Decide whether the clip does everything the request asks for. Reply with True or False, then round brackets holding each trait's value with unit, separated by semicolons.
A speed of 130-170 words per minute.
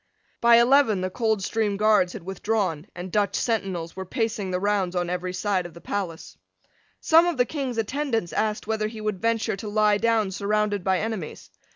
False (185 wpm)